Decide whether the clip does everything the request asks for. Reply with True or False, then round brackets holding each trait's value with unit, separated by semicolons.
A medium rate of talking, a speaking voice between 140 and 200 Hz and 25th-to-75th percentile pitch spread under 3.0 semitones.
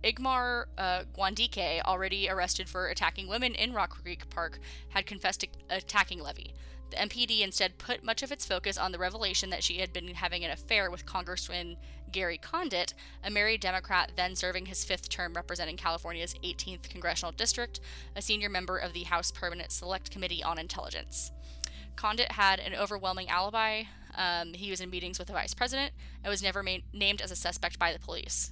True (185 wpm; 185 Hz; 2.6 semitones)